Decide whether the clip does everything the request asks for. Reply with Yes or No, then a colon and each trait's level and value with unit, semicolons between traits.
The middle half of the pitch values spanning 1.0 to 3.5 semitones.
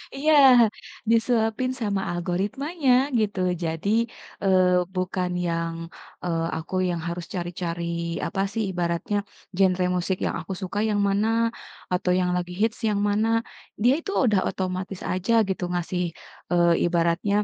Yes: average, 3.2 semitones